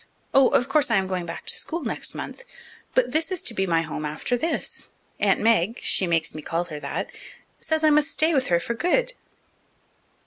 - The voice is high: Yes, high, 230 Hz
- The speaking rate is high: Yes, fast, 210 wpm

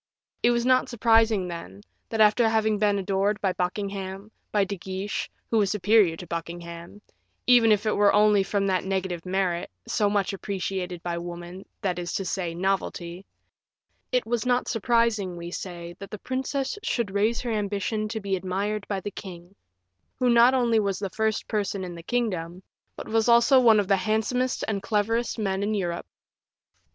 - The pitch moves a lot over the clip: No, average, 3.0 semitones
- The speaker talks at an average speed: Yes, average, 175 wpm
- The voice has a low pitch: No, high, 200 Hz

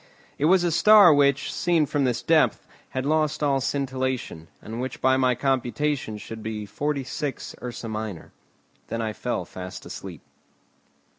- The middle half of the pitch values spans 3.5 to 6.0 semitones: Yes, average, 4.4 semitones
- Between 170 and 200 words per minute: No, average, 150 wpm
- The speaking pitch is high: No, low, 130 Hz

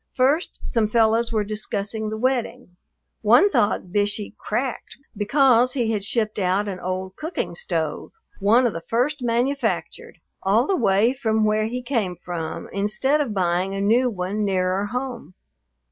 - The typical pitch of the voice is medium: No, high, 220 Hz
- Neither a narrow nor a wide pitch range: Yes, average, 3.9 semitones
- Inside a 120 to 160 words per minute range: Yes, average, 155 wpm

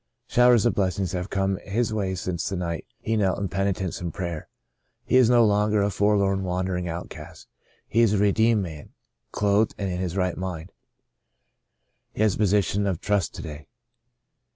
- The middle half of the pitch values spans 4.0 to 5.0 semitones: No, narrow, 2.5 semitones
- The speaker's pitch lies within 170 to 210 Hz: No, very low, 95 Hz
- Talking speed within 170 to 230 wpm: Yes, average, 180 wpm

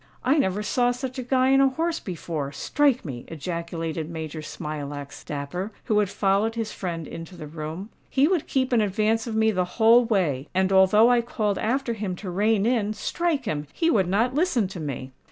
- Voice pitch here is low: No, high, 205 Hz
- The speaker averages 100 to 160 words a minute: No, average, 190 wpm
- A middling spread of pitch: No, wide, 6.6 semitones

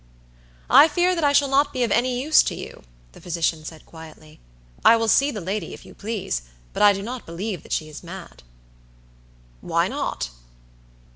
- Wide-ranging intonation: Yes, wide, 7.8 semitones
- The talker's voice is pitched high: Yes, high, 210 Hz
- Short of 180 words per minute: No, average, 190 wpm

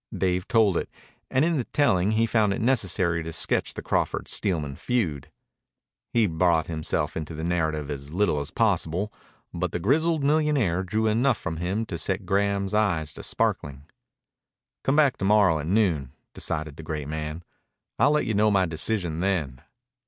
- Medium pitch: No, very low, 90 Hz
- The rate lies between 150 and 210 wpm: Yes, average, 175 wpm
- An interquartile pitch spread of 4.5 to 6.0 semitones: Yes, wide, 5.5 semitones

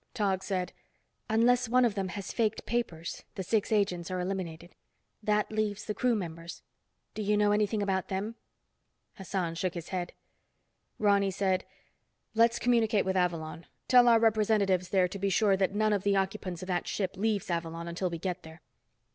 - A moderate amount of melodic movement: Yes, average, 3.0 semitones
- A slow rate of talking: No, average, 175 wpm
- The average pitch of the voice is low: No, high, 195 Hz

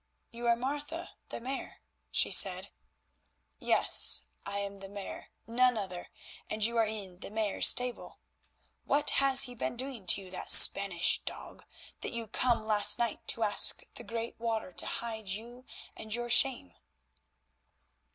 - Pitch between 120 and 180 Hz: No, high, 230 Hz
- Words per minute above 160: No, average, 155 wpm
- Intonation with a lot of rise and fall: No, average, 3.4 semitones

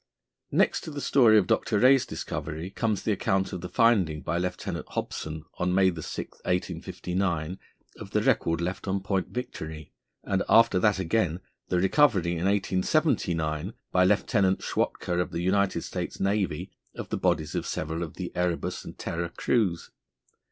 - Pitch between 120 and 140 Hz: No, very low, 95 Hz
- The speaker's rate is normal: Yes, average, 160 wpm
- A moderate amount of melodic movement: Yes, average, 3.1 semitones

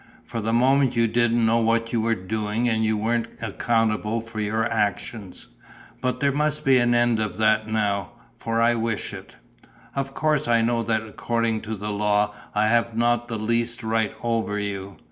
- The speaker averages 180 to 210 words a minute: Yes, average, 185 wpm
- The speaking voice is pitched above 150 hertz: No, low, 115 Hz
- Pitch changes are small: Yes, narrow, 1.6 semitones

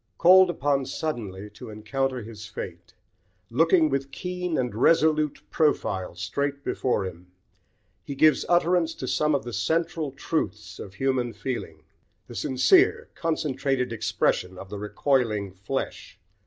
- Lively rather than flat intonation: Yes, wide, 6.7 semitones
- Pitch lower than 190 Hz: Yes, low, 135 Hz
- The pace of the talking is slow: Yes, slow, 130 wpm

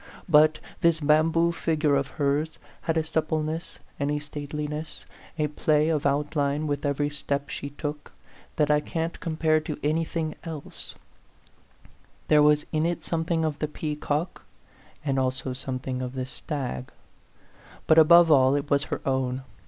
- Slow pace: No, average, 165 wpm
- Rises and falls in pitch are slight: Yes, narrow, 1.8 semitones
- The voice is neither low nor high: Yes, medium, 150 Hz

